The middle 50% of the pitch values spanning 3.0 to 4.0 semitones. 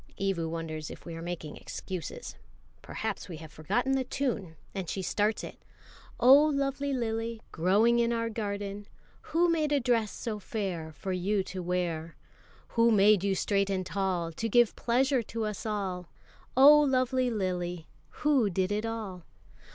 No: average, 4.7 semitones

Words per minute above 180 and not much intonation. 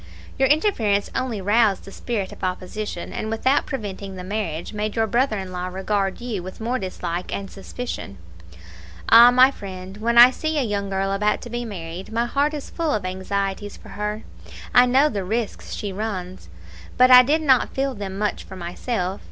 No: average, 190 wpm; average, 4.3 semitones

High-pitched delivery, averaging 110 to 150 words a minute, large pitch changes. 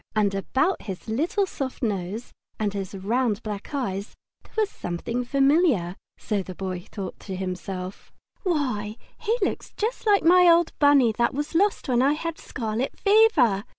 No: high, 240 Hz; average, 165 wpm; wide, 8.3 semitones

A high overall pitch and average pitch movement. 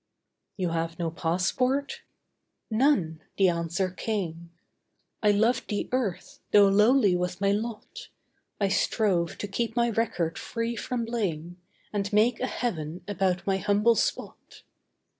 Yes: high, 200 Hz; average, 4.5 semitones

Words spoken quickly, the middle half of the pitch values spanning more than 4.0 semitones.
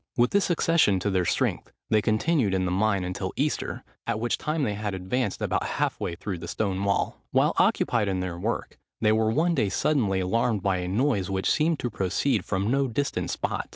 Yes: fast, 210 wpm; average, 5.0 semitones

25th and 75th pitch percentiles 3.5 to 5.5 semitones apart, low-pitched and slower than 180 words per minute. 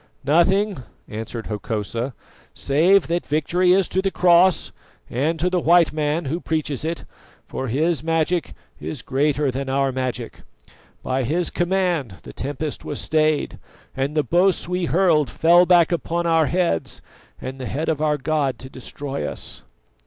No: average, 4.4 semitones; medium, 155 Hz; average, 155 wpm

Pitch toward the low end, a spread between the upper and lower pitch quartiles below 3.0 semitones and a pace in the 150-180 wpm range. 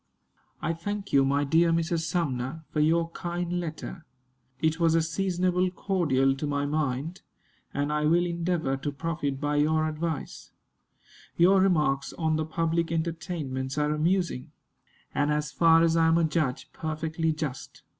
No: medium, 160 Hz; narrow, 2.4 semitones; average, 155 wpm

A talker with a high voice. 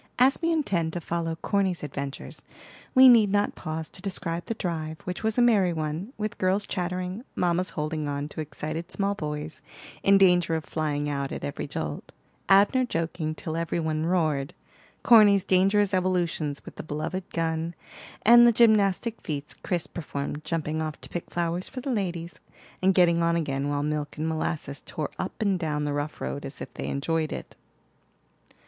No: medium, 170 Hz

